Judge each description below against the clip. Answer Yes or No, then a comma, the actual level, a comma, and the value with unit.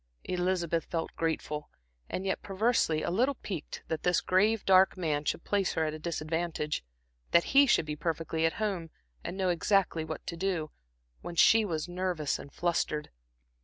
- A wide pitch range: No, average, 3.2 semitones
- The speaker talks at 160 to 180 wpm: Yes, average, 170 wpm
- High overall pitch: No, medium, 170 Hz